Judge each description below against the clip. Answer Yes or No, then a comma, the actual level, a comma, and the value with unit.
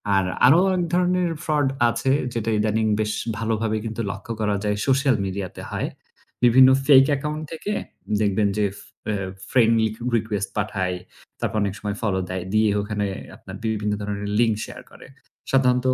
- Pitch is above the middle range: No, low, 110 Hz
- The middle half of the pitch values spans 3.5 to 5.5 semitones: Yes, average, 4.2 semitones